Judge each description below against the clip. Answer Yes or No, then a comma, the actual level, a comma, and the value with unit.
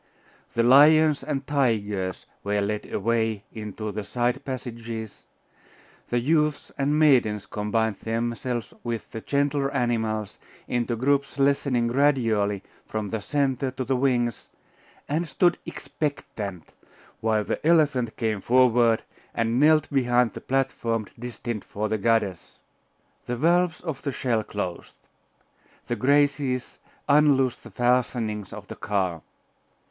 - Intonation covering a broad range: No, average, 4.1 semitones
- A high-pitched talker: No, low, 120 Hz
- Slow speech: Yes, slow, 125 wpm